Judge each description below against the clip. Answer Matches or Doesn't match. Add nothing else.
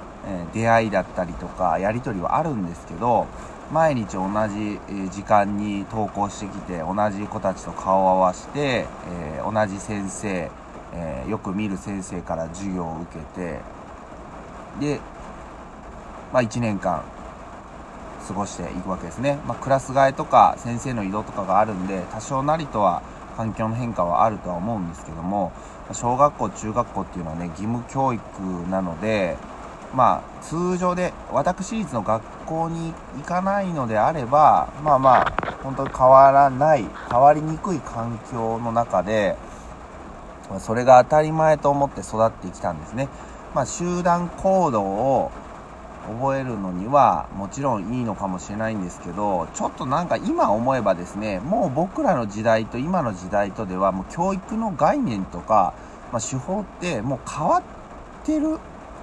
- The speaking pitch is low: Matches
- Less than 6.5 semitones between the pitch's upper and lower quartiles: Matches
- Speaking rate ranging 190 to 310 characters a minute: Matches